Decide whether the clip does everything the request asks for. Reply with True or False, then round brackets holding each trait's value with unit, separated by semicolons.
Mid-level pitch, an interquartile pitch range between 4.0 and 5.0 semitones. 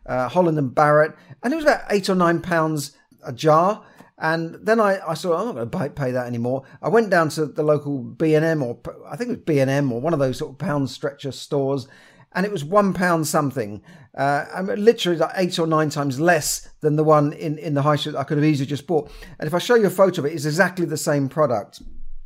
False (155 Hz; 3.6 semitones)